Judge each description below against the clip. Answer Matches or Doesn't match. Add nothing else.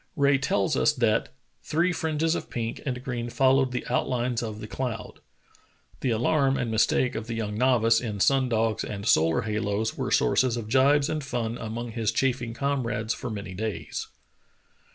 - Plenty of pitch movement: Doesn't match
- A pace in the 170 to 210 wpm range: Matches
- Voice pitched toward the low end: Matches